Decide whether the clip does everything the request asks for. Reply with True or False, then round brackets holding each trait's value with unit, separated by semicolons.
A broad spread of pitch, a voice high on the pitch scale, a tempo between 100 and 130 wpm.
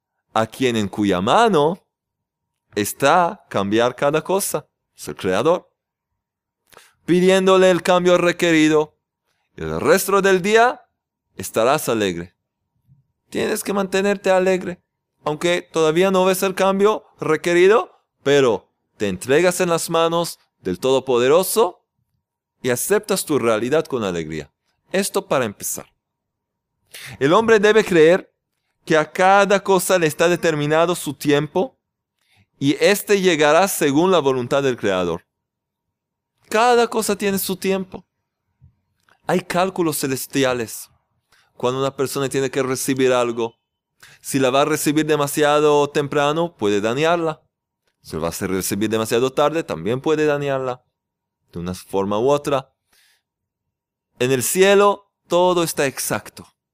False (6.2 semitones; 155 Hz; 125 wpm)